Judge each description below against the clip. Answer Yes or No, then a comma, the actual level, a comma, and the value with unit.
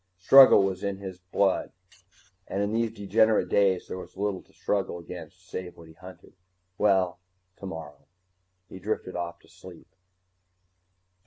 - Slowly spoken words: No, average, 145 wpm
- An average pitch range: No, narrow, 2.1 semitones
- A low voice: Yes, very low, 95 Hz